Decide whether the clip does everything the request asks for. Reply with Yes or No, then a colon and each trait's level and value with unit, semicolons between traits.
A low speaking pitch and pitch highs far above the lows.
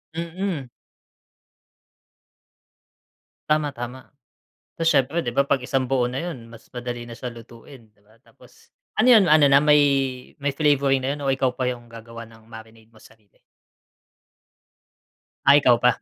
No: low, 130 Hz; average, 3.6 semitones